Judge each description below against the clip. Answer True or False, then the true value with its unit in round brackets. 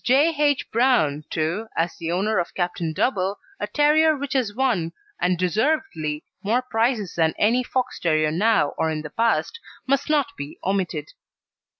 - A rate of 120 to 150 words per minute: False (165 wpm)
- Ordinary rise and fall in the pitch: False (7.9 semitones)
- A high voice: True (215 Hz)